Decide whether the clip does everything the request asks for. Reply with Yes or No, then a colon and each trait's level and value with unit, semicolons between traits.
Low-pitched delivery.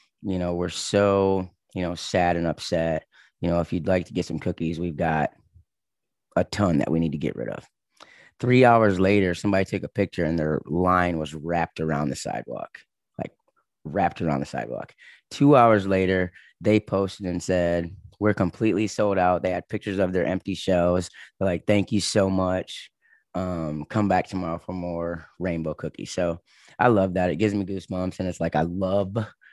Yes: very low, 90 Hz